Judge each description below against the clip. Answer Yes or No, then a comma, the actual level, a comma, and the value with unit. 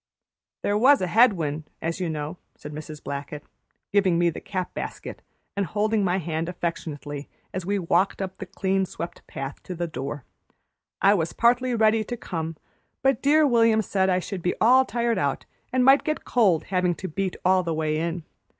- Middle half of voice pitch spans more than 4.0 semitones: Yes, average, 5.0 semitones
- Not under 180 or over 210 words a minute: Yes, average, 190 wpm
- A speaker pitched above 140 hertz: Yes, medium, 185 Hz